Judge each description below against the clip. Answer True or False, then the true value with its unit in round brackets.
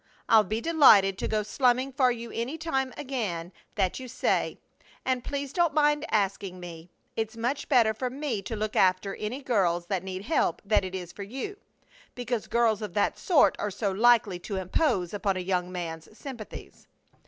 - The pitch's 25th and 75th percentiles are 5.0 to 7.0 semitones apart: True (5.3 semitones)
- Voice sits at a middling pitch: False (220 Hz)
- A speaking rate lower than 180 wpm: False (185 wpm)